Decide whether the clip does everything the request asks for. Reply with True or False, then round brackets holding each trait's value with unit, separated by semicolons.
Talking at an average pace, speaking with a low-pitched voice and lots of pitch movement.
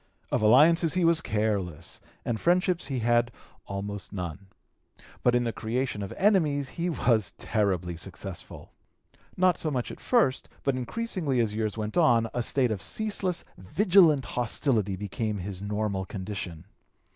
True (145 wpm; 115 Hz; 7.3 semitones)